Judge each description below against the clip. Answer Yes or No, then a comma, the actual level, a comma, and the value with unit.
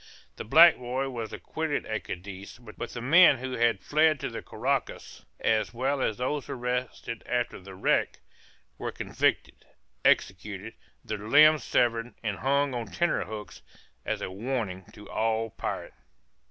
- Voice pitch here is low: Yes, low, 120 Hz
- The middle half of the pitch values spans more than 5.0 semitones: No, average, 3.8 semitones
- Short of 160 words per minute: Yes, average, 150 wpm